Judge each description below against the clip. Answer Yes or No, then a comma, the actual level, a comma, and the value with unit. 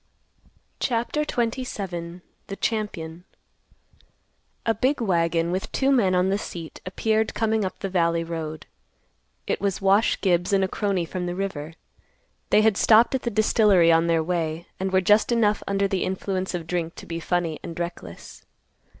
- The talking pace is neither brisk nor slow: Yes, average, 165 wpm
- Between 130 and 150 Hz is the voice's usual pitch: No, high, 190 Hz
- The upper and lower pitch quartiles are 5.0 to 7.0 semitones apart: No, average, 4.0 semitones